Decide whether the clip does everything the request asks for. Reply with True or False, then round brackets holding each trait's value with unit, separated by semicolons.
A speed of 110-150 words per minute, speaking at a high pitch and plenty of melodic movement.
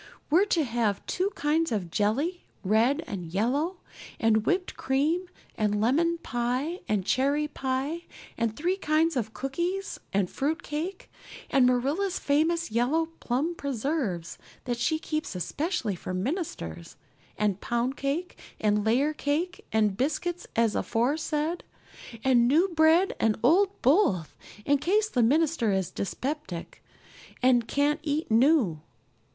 True (135 wpm; 275 Hz; 6.4 semitones)